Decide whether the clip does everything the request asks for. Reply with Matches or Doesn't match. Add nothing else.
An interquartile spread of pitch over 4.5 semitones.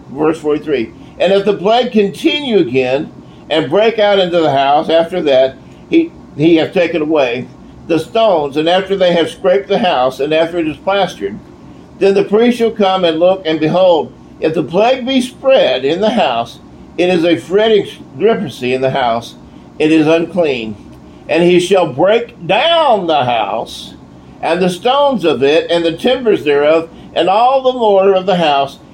Matches